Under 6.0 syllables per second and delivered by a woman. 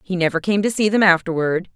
No: 6.1 syllables/s; female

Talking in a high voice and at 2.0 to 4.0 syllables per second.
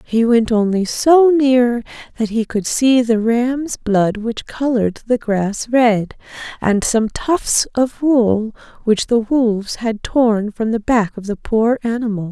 Yes: high, 230 Hz; 3.7 syllables/s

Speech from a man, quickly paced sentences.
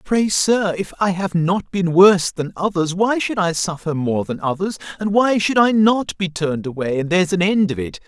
Yes: male; fast, 230 wpm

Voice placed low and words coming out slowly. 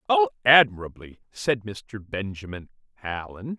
Yes: low, 115 Hz; slow, 100 wpm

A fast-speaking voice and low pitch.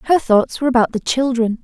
No: fast, 220 wpm; high, 245 Hz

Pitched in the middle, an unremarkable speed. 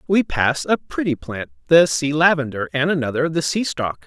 Yes: medium, 150 Hz; average, 190 wpm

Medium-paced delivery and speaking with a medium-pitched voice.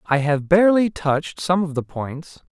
Yes: average, 190 wpm; medium, 160 Hz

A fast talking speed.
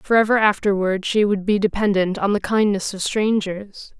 No: average, 165 wpm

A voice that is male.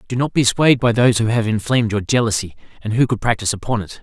Yes: male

